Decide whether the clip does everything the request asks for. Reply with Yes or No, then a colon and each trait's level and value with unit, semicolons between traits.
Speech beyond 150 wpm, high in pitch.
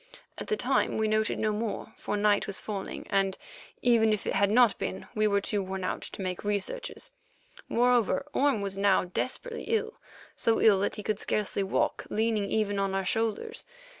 Yes: average, 185 wpm; high, 210 Hz